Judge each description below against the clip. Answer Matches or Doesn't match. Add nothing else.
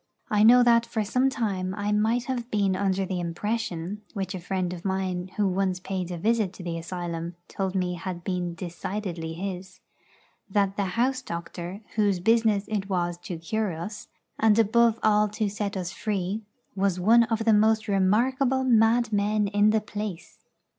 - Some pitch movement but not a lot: Matches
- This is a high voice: Matches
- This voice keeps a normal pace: Matches